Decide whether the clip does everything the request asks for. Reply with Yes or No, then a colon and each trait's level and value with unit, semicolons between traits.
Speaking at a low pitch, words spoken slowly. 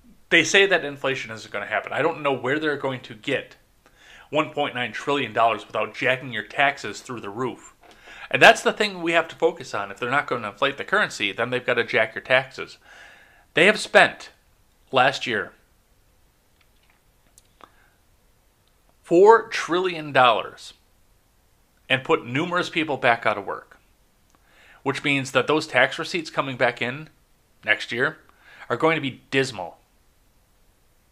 No: low, 130 Hz; average, 155 wpm